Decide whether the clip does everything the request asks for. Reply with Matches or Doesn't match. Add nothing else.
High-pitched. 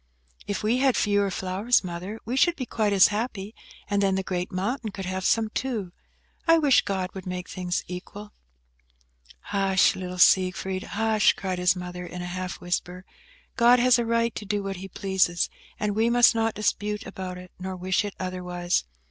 Matches